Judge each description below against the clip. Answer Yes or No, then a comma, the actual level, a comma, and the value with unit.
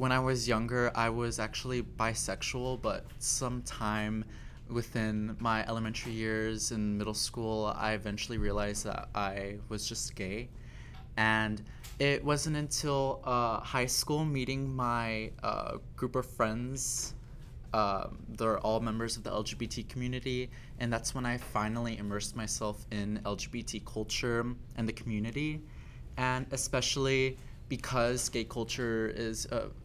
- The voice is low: Yes, low, 115 Hz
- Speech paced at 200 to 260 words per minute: No, slow, 135 wpm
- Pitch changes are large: No, narrow, 2.6 semitones